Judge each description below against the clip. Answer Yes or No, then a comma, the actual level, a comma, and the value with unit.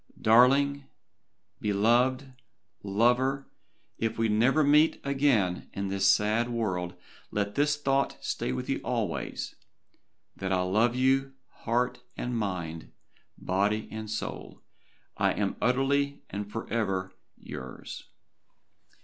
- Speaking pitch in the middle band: No, low, 115 Hz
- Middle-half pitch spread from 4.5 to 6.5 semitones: Yes, average, 5.0 semitones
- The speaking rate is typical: No, slow, 110 wpm